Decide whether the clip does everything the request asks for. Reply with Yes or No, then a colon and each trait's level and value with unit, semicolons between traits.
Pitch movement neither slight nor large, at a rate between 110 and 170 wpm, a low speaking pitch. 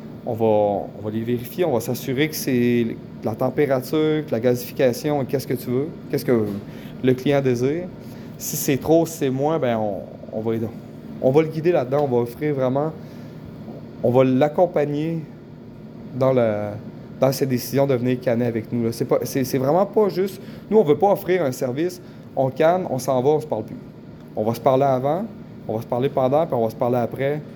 No: average, 3.7 semitones; average, 210 wpm; low, 130 Hz